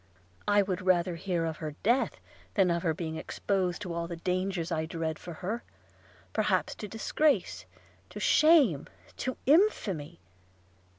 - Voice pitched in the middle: Yes, medium, 180 Hz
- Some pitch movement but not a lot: Yes, average, 3.8 semitones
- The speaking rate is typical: Yes, average, 150 wpm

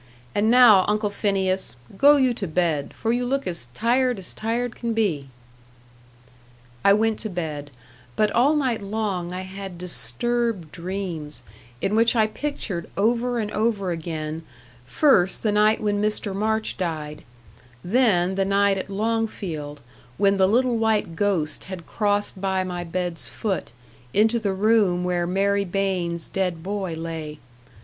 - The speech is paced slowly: No, average, 150 wpm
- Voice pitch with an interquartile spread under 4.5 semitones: Yes, average, 4.0 semitones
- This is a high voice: Yes, high, 195 Hz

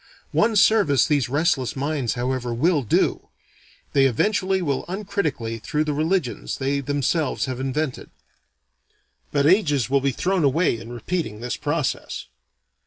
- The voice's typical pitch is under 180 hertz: Yes, medium, 140 Hz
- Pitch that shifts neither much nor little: Yes, average, 4.7 semitones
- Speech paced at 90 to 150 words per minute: Yes, slow, 135 wpm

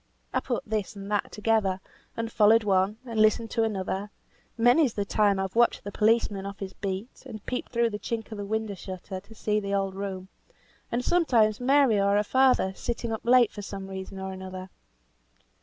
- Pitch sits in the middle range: No, high, 210 Hz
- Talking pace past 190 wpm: Yes, average, 200 wpm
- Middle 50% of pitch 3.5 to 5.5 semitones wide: No, average, 2.7 semitones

